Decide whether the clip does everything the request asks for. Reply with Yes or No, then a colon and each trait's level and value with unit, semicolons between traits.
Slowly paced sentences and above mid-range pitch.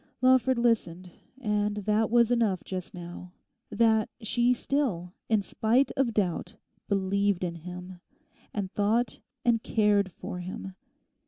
Yes: slow, 120 wpm; high, 210 Hz